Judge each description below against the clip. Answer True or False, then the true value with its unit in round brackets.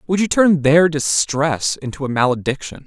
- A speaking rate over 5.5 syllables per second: False (4.9 syllables/s)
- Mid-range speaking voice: True (150 Hz)